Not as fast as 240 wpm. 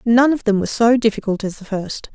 No: fast, 250 wpm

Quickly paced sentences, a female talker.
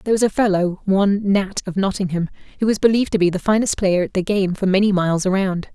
Yes: fast, 240 wpm; female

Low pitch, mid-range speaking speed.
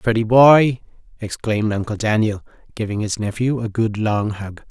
Yes: low, 110 Hz; average, 155 wpm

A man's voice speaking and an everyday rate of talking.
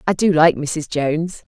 No: female; average, 195 wpm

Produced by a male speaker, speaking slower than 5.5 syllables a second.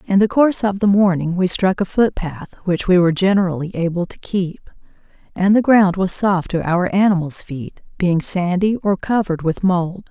No: female; 5.0 syllables/s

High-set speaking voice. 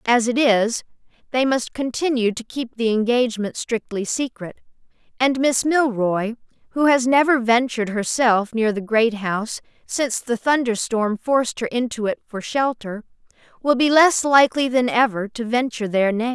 Yes: high, 240 Hz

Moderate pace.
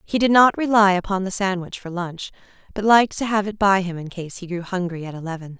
No: fast, 245 wpm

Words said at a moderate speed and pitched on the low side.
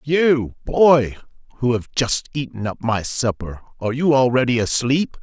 Yes: average, 150 wpm; low, 125 Hz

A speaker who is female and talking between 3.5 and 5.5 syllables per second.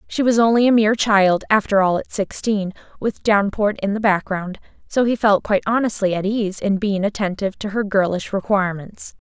Yes: female; 5.4 syllables/s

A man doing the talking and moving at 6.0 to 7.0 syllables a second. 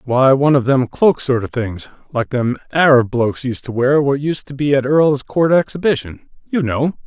No: male; 5.0 syllables/s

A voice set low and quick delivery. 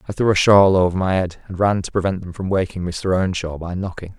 Yes: very low, 95 Hz; fast, 260 wpm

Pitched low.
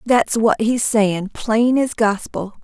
No: high, 220 Hz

